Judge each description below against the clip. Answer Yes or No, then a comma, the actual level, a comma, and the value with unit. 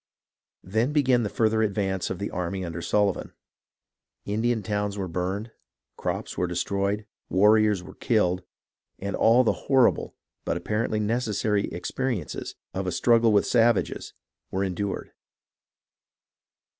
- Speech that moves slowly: Yes, slow, 125 wpm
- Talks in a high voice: No, low, 105 Hz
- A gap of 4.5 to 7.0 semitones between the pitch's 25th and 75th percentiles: No, average, 2.9 semitones